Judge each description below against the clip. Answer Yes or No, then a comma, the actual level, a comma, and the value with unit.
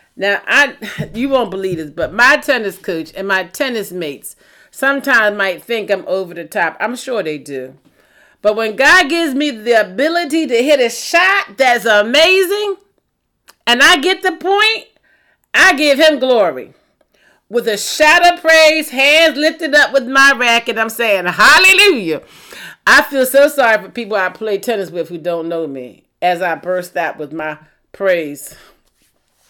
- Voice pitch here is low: No, high, 235 Hz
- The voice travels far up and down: Yes, wide, 8.0 semitones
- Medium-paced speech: Yes, average, 165 wpm